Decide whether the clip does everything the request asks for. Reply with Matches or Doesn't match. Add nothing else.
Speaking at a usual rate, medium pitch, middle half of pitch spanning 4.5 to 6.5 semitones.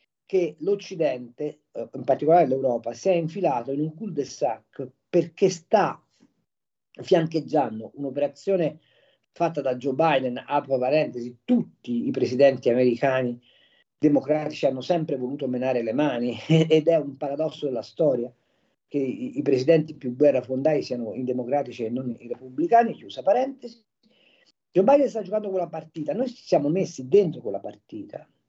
Matches